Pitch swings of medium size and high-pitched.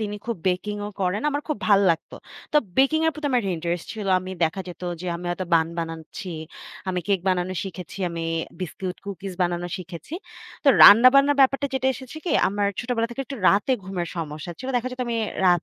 No: wide, 5.9 semitones; high, 195 Hz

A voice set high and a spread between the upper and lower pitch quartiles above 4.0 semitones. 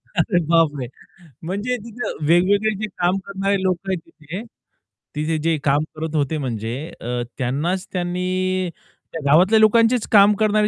No: medium, 180 Hz; average, 4.4 semitones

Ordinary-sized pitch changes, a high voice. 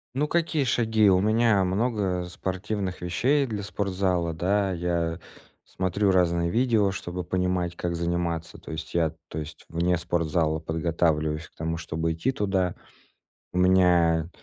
No: average, 3.1 semitones; very low, 90 Hz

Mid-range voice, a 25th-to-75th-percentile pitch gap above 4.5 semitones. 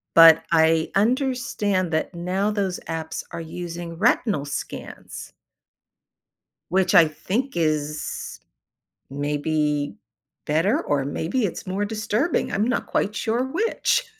Yes: medium, 175 Hz; average, 5.2 semitones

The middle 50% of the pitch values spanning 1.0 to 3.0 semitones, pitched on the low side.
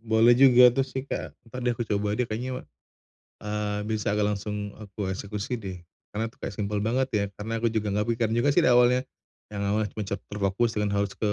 Yes: narrow, 2.6 semitones; low, 110 Hz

